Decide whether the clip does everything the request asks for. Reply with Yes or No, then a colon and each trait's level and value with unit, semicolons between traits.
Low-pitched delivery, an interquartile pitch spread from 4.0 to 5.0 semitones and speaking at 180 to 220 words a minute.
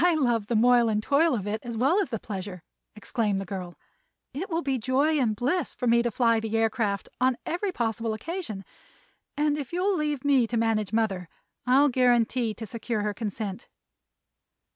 No: high, 235 Hz; average, 4.5 semitones; average, 185 wpm